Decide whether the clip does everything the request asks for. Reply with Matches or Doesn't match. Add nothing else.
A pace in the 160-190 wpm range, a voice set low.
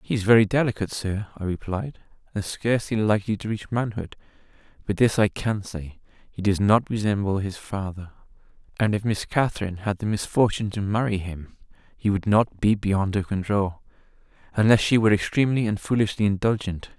Matches